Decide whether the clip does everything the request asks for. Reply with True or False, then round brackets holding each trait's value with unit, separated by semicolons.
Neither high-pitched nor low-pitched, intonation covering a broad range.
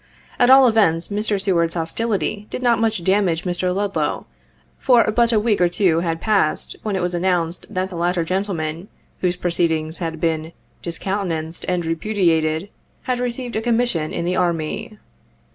False (180 Hz; 4.3 semitones)